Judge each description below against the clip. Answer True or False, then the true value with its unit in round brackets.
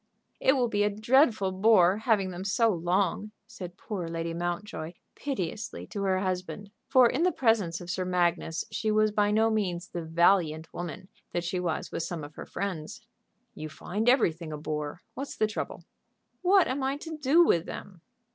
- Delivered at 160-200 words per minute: True (185 wpm)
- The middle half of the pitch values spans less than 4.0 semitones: False (4.3 semitones)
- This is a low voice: False (190 Hz)